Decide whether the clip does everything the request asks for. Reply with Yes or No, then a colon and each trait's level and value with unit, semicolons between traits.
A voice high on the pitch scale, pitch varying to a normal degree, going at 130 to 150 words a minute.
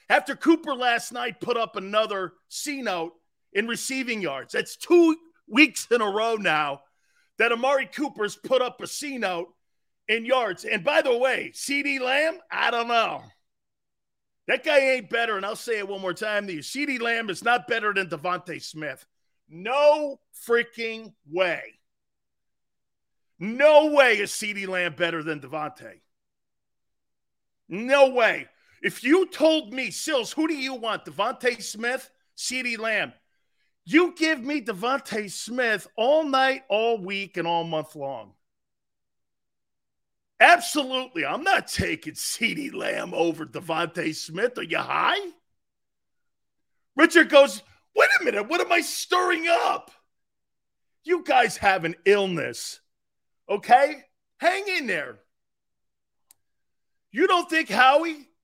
No: high, 240 Hz; wide, 6.9 semitones; slow, 135 wpm